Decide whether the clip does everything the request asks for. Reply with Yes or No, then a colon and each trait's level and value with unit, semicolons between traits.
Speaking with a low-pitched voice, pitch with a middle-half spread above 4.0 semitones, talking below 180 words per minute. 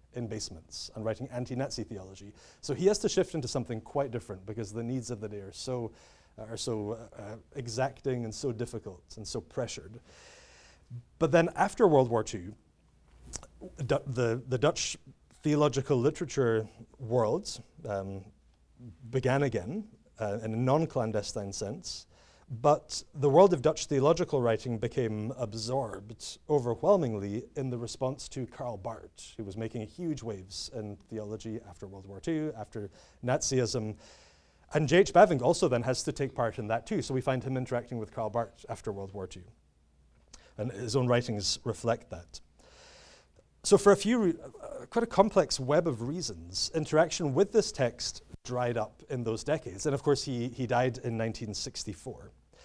Yes: low, 120 Hz; average, 4.6 semitones; average, 165 wpm